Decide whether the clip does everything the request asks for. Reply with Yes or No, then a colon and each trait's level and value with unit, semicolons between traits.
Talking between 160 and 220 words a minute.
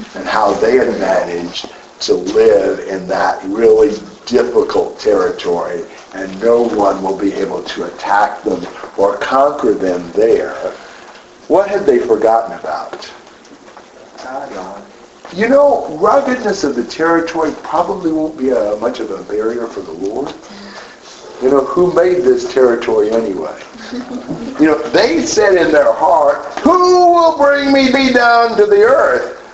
No: average, 145 wpm